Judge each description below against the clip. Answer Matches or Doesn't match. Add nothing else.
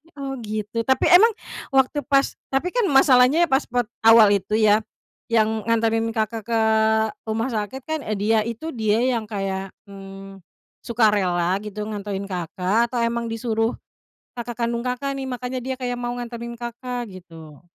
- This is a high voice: Matches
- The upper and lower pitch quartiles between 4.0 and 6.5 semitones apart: Doesn't match